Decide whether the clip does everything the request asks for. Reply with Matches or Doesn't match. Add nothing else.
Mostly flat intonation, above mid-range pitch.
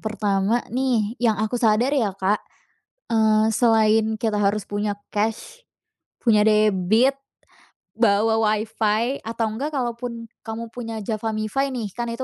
Matches